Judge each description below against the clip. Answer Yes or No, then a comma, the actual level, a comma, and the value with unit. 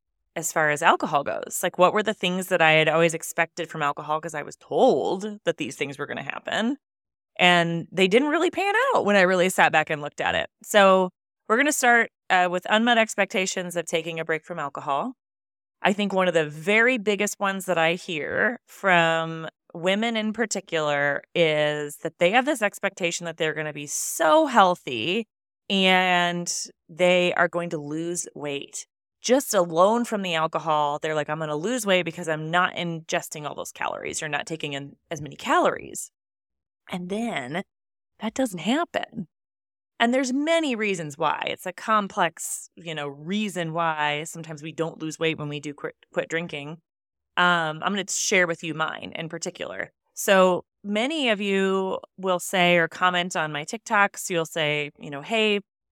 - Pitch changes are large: No, average, 4.3 semitones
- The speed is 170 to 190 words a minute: Yes, average, 185 wpm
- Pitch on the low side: No, medium, 175 Hz